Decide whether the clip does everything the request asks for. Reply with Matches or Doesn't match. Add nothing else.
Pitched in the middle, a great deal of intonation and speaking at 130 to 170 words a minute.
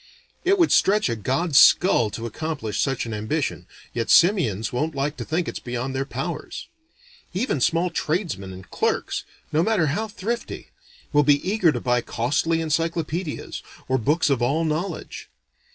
Matches